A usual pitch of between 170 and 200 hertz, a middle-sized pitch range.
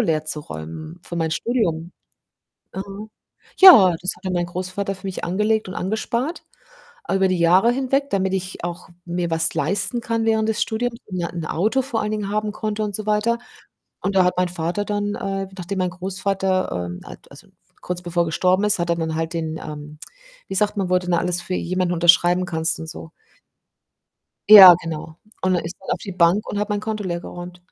Yes: medium, 185 Hz; average, 3.3 semitones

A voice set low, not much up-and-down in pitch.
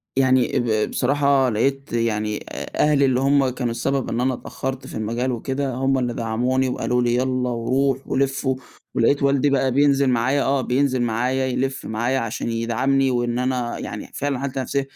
Yes: low, 130 Hz; narrow, 2.2 semitones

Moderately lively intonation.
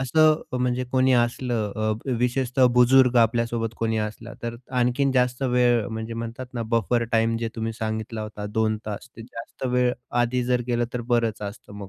No: narrow, 1.9 semitones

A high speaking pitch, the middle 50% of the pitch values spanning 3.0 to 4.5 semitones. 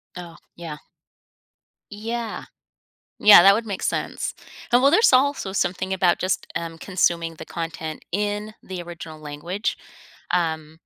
No: medium, 180 Hz; average, 3.9 semitones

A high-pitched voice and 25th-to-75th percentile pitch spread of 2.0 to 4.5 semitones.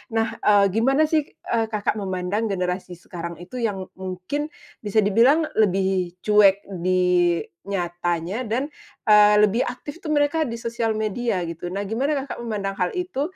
Yes: high, 210 Hz; average, 4.2 semitones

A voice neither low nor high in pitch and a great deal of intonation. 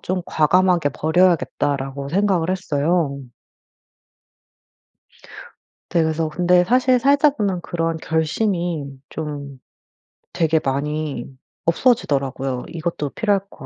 No: medium, 165 Hz; average, 4.1 semitones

